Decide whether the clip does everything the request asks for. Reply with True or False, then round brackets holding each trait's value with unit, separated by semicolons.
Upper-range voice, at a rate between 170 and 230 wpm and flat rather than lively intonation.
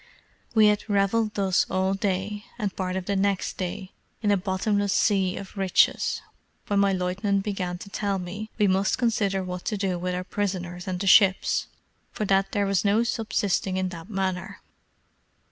True (195 Hz; 180 wpm; 1.6 semitones)